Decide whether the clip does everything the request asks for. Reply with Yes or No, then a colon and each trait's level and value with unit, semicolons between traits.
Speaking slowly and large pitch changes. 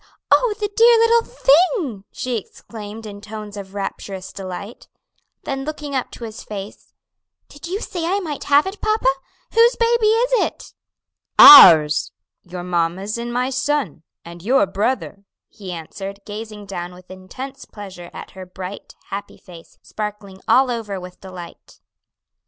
No: average, 150 wpm; wide, 7.2 semitones